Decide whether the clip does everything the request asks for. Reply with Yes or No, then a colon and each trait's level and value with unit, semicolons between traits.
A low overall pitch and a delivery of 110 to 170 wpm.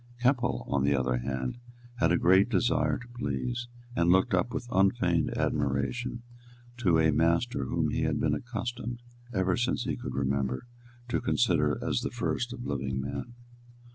Yes: very low, 95 Hz; average, 165 wpm